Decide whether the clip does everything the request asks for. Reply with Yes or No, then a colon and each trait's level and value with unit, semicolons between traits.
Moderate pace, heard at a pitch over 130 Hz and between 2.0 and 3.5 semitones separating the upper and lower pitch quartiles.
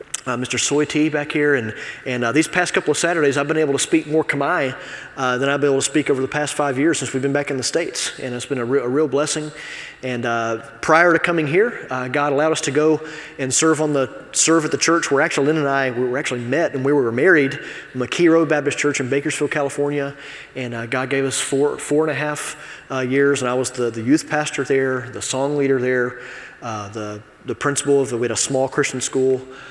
No: fast, 250 wpm; medium, 140 Hz; average, 2.8 semitones